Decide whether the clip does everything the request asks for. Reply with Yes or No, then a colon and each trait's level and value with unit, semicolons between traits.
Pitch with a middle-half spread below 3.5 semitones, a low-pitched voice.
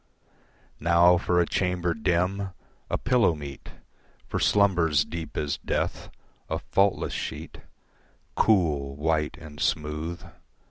Yes: average, 3.1 semitones; very low, 85 Hz